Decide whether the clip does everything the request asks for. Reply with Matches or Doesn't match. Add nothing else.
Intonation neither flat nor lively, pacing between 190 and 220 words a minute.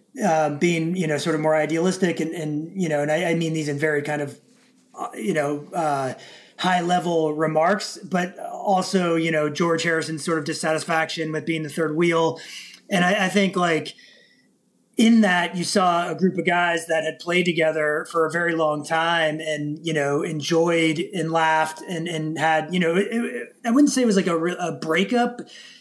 Doesn't match